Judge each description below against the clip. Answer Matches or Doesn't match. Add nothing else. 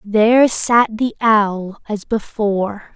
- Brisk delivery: Doesn't match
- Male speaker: Doesn't match